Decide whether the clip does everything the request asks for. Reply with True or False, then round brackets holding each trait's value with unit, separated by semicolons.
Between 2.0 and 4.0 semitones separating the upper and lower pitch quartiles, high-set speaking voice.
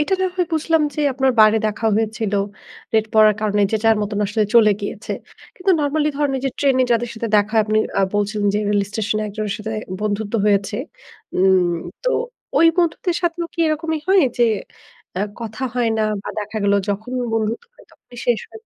False (5.4 semitones; 220 Hz)